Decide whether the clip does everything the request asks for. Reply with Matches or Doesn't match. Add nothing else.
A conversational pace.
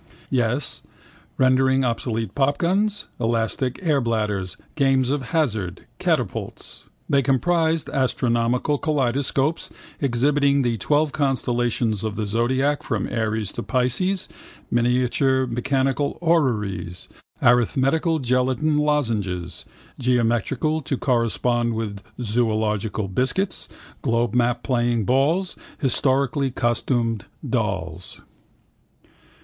Doesn't match